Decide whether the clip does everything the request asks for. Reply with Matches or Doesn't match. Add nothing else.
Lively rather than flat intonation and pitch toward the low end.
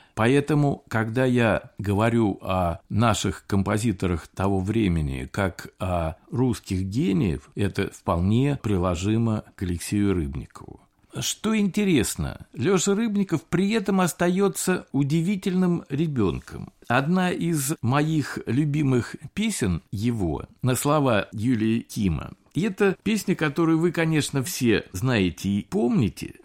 Matches